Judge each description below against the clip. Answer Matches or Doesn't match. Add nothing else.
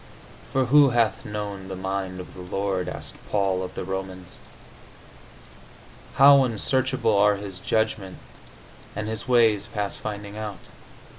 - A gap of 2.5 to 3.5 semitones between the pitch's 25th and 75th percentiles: Matches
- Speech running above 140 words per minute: Doesn't match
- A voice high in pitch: Doesn't match